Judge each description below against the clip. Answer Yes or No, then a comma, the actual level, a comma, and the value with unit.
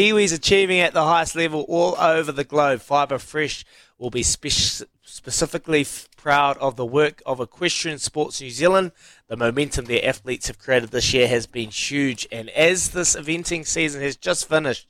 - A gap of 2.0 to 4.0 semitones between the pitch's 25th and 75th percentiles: No, average, 4.6 semitones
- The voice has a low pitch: No, medium, 145 Hz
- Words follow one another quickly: No, average, 180 wpm